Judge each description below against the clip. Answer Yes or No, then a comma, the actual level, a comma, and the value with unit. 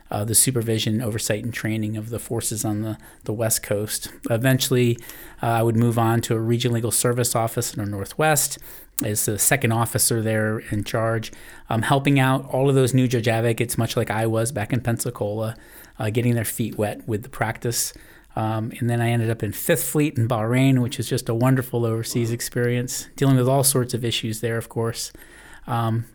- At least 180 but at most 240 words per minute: Yes, average, 200 wpm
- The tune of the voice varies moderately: No, narrow, 1.9 semitones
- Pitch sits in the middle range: No, low, 115 Hz